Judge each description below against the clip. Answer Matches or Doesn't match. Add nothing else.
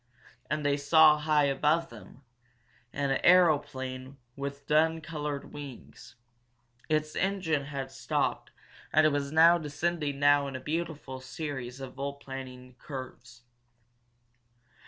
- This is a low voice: Doesn't match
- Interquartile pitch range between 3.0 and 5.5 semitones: Doesn't match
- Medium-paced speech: Doesn't match